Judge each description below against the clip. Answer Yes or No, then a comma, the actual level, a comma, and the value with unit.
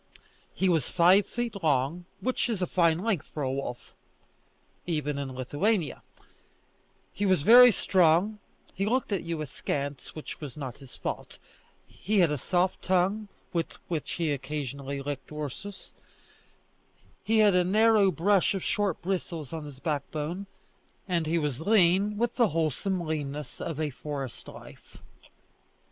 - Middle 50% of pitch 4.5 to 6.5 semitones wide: Yes, average, 5.1 semitones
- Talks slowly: No, average, 150 wpm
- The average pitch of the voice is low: No, medium, 170 Hz